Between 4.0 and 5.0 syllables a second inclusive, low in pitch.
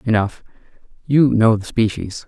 Yes: 4.3 syllables/s; low, 115 Hz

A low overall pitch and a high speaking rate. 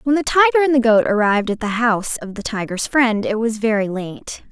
No: high, 230 Hz; fast, 240 wpm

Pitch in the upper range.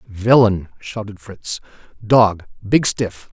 No: low, 105 Hz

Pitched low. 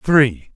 Yes: low, 125 Hz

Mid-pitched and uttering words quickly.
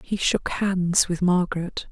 No: medium, 180 Hz; average, 155 wpm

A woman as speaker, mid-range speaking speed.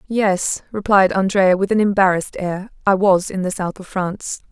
Yes: female; average, 185 wpm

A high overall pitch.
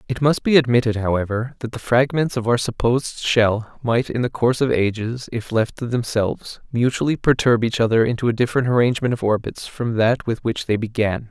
No: low, 120 Hz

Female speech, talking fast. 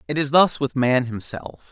No: male; fast, 210 wpm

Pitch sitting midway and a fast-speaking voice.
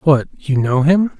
No: medium, 150 Hz; average, 150 wpm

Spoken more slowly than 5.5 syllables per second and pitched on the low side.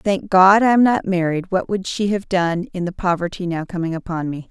No: 5.3 syllables/s; medium, 185 Hz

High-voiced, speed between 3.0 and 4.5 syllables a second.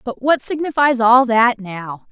Yes: high, 240 Hz; 4.0 syllables/s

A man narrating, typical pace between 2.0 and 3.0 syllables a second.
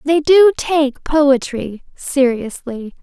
No: female; 2.9 syllables/s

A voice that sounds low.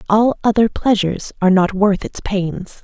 No: high, 200 Hz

